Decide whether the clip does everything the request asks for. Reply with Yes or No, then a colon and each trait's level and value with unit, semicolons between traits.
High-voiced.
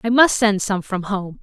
Yes: high, 205 Hz